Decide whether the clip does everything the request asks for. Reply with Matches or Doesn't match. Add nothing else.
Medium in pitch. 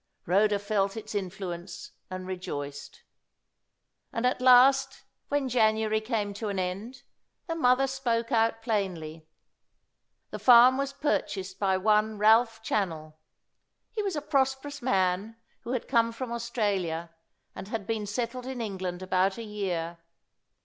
Doesn't match